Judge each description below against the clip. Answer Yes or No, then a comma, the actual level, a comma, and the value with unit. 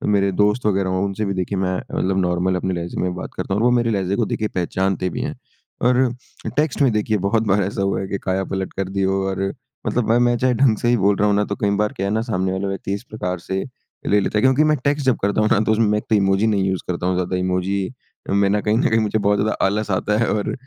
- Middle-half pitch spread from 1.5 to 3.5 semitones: Yes, narrow, 2.4 semitones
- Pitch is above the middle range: No, low, 100 Hz